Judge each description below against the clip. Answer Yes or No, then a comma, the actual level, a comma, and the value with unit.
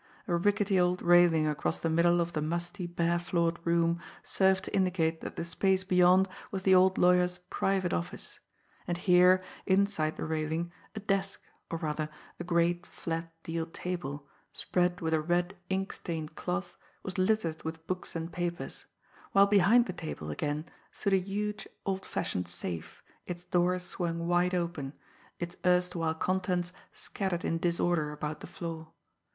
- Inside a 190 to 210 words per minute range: No, average, 160 wpm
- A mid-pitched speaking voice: Yes, medium, 175 Hz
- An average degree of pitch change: No, narrow, 2.1 semitones